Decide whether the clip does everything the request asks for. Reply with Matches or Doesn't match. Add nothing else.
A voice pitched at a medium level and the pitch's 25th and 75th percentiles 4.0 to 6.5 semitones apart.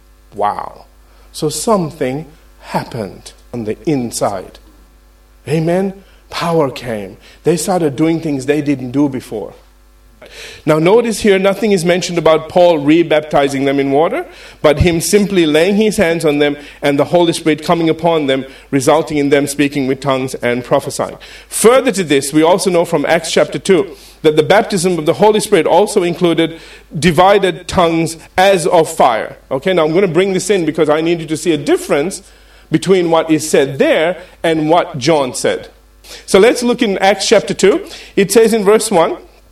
Matches